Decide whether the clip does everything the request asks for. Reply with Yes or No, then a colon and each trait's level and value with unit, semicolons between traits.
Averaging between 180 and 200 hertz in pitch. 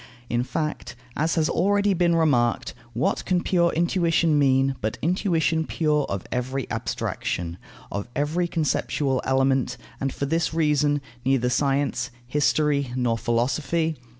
No: medium, 145 Hz